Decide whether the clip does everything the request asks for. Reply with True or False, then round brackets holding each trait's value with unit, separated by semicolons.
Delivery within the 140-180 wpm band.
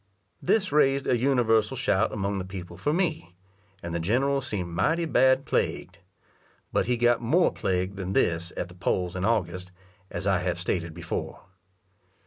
True (165 wpm)